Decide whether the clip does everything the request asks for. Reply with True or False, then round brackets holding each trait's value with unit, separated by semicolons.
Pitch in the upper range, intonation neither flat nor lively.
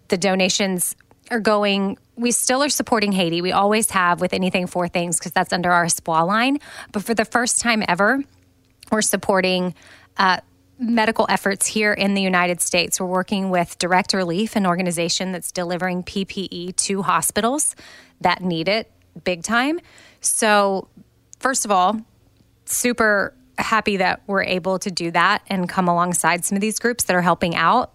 True (195 Hz; 3.3 semitones)